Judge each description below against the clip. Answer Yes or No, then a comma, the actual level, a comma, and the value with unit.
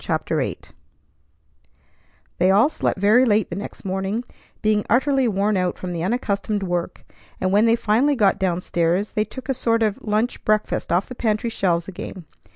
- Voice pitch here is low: No, high, 210 Hz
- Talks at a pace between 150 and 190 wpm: Yes, average, 180 wpm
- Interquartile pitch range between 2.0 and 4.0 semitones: Yes, average, 3.5 semitones